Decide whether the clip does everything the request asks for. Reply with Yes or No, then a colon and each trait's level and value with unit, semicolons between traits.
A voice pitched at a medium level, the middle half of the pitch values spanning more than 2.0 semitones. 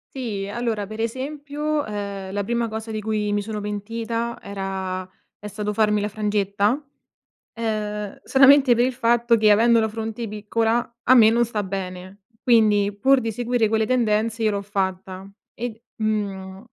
No: high, 215 Hz; narrow, 2.5 semitones